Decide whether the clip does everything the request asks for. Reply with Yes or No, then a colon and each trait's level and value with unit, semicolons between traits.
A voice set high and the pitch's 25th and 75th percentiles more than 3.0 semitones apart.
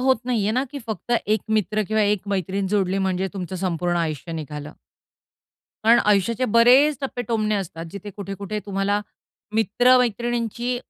Yes: high, 205 Hz; average, 3.7 semitones